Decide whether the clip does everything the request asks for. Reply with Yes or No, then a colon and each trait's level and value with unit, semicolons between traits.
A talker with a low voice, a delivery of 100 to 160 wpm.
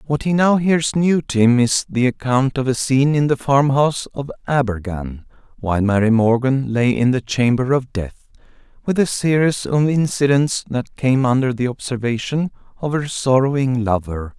No: low, 130 Hz; average, 175 wpm